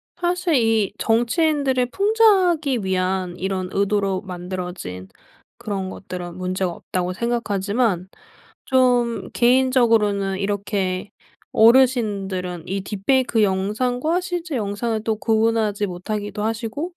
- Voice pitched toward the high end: Yes, high, 215 Hz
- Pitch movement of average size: Yes, average, 4.6 semitones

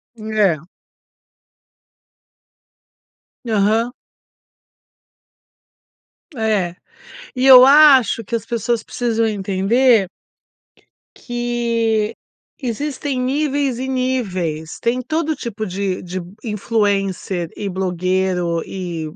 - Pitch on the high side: Yes, high, 220 Hz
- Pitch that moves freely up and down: No, average, 4.8 semitones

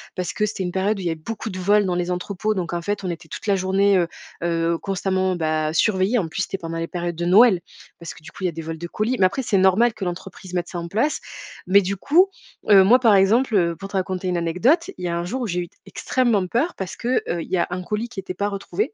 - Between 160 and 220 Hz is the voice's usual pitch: Yes, high, 190 Hz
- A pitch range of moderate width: Yes, average, 3.1 semitones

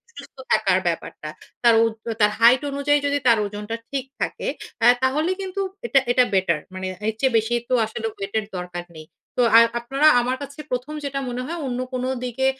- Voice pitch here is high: Yes, high, 240 Hz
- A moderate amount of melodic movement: Yes, average, 4.5 semitones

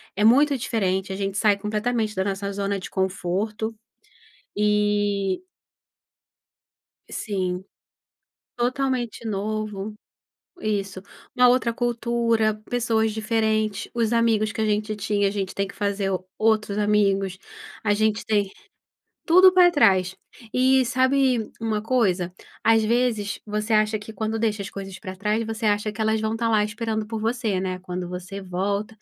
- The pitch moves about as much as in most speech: No, narrow, 2.3 semitones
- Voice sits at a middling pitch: No, high, 215 Hz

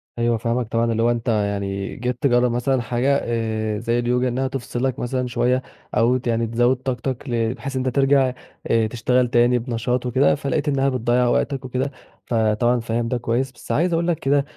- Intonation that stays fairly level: Yes, narrow, 2.0 semitones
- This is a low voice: Yes, low, 120 Hz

